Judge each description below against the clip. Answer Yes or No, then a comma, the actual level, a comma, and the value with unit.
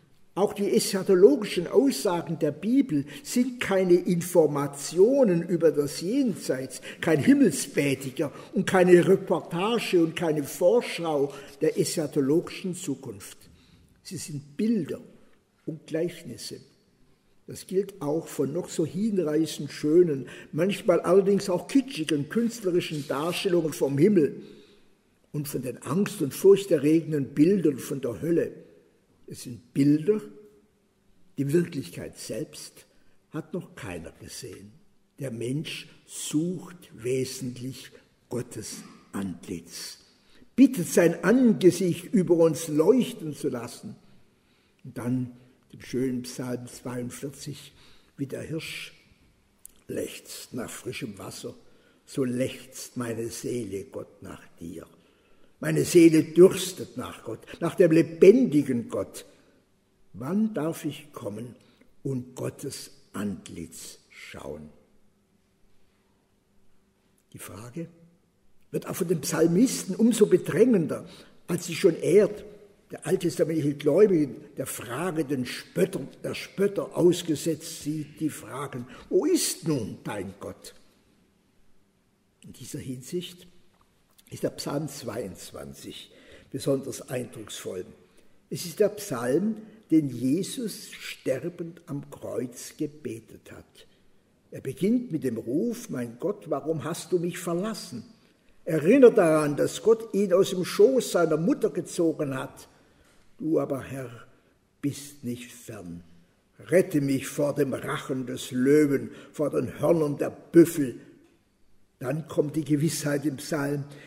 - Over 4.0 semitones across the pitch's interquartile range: Yes, average, 5.3 semitones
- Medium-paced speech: No, slow, 110 wpm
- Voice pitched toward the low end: No, medium, 160 Hz